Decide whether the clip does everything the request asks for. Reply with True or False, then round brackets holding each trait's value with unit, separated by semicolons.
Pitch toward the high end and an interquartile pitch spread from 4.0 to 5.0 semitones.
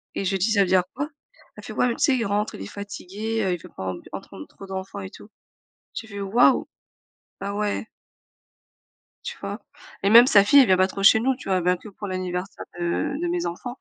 False (200 Hz; 3.2 semitones)